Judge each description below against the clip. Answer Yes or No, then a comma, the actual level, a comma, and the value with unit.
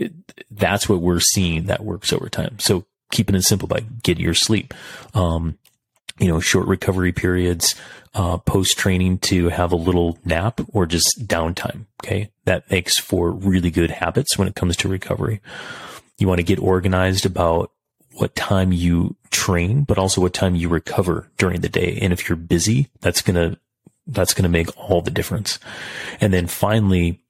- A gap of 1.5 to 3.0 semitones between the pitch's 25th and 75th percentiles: Yes, narrow, 2.6 semitones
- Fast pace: No, average, 180 wpm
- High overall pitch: No, very low, 95 Hz